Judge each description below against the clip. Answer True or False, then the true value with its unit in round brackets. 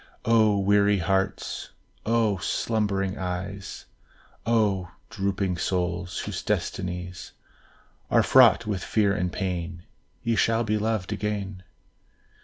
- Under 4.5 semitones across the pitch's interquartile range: True (2.6 semitones)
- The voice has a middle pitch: False (100 Hz)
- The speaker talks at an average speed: False (105 wpm)